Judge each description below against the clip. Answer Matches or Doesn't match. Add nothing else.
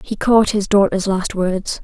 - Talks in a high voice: Matches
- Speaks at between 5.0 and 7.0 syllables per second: Doesn't match